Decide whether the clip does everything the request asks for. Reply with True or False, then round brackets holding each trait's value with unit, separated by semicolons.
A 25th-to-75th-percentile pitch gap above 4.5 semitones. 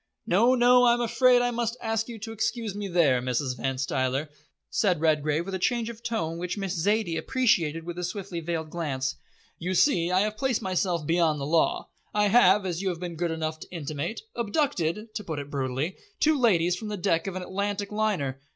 True (5.3 semitones)